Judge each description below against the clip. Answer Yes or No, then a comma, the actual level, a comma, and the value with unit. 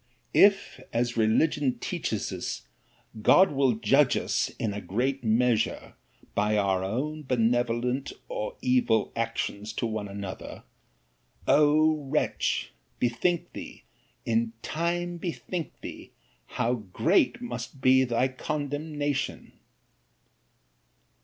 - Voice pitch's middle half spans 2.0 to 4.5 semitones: No, wide, 5.4 semitones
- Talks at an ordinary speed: No, slow, 100 wpm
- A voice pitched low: Yes, low, 130 Hz